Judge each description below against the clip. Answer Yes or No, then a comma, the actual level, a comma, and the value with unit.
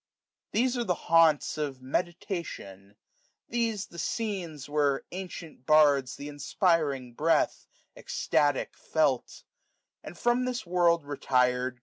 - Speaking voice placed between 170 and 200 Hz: No, medium, 155 Hz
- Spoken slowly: Yes, slow, 110 wpm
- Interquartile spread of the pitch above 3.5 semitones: Yes, average, 4.8 semitones